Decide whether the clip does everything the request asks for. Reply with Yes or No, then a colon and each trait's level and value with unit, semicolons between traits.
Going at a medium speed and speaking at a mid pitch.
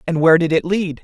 No: fast, 290 wpm; medium, 170 Hz